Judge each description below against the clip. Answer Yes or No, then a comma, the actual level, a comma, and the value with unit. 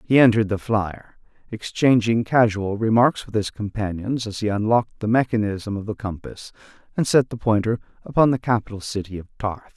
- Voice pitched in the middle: No, low, 110 Hz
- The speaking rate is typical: Yes, average, 170 wpm